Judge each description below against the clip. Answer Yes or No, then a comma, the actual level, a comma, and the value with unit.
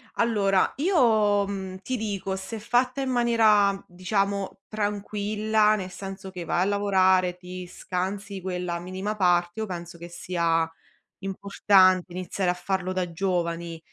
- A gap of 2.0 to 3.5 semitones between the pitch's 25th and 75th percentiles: Yes, narrow, 2.4 semitones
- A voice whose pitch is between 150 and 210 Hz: Yes, high, 190 Hz